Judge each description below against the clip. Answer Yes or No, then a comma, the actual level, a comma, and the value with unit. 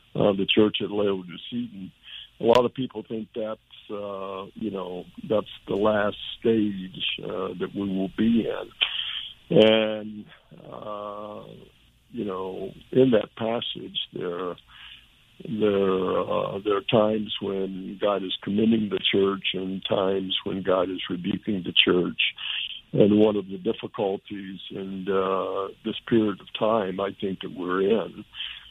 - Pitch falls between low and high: No, low, 100 Hz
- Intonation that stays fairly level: Yes, narrow, 2.2 semitones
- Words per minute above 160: No, average, 140 wpm